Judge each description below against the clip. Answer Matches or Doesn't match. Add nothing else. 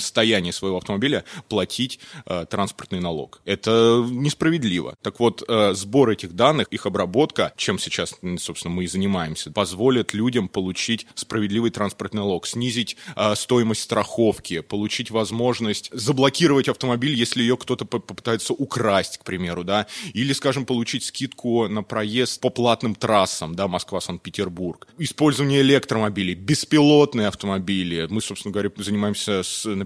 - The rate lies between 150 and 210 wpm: Doesn't match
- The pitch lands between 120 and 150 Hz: Doesn't match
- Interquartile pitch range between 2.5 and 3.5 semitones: Doesn't match